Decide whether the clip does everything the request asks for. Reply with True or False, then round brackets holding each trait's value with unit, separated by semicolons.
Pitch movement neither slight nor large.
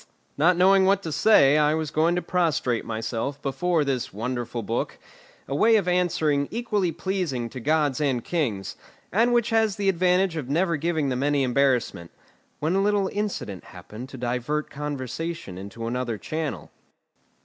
False (6.2 semitones)